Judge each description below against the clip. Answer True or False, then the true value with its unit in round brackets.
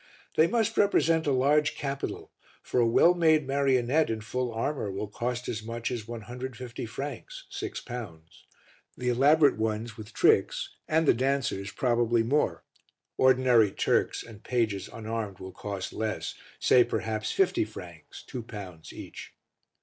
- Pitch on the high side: False (120 Hz)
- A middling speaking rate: True (145 wpm)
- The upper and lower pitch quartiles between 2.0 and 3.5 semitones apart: False (4.2 semitones)